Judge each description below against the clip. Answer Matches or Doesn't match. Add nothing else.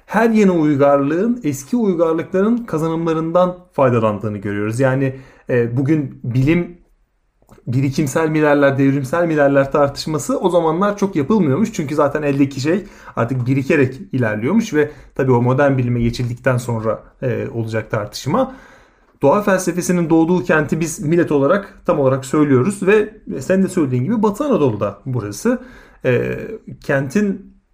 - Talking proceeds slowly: Doesn't match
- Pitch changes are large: Matches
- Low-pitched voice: Doesn't match